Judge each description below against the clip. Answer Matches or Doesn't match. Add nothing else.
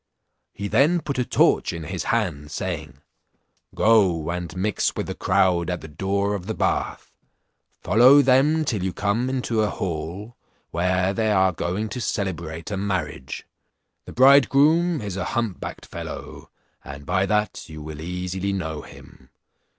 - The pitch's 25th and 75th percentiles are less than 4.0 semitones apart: Doesn't match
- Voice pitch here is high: Doesn't match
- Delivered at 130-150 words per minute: Doesn't match